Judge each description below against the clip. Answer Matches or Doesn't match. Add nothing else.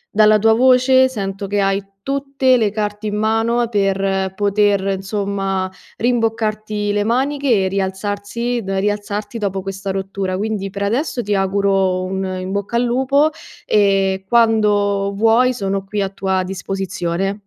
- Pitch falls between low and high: Doesn't match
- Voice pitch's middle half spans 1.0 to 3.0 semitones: Matches